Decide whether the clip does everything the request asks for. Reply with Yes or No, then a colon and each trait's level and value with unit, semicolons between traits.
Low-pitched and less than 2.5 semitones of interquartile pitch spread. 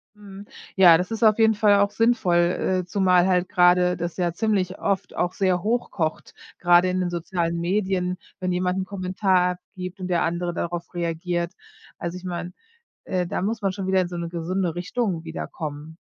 No: medium, 180 Hz; narrow, 1.7 semitones